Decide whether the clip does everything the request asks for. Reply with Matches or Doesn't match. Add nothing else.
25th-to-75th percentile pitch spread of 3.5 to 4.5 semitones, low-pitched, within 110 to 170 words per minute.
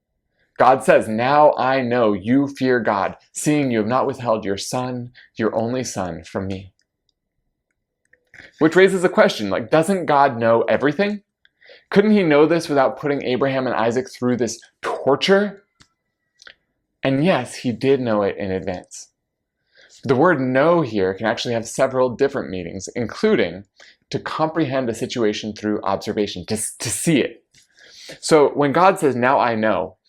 Doesn't match